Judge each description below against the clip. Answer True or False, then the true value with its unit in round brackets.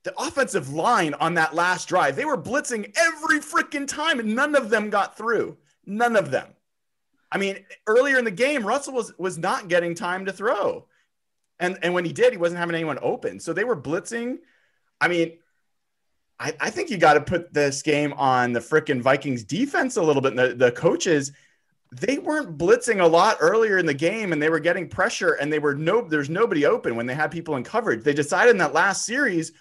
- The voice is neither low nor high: True (180 Hz)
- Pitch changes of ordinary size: False (7.7 semitones)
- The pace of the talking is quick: True (215 wpm)